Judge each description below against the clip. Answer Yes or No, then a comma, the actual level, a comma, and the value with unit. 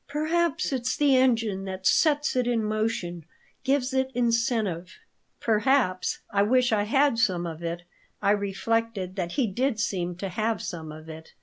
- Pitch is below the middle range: No, high, 220 Hz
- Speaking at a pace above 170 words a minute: No, average, 165 wpm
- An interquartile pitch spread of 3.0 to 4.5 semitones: No, wide, 5.6 semitones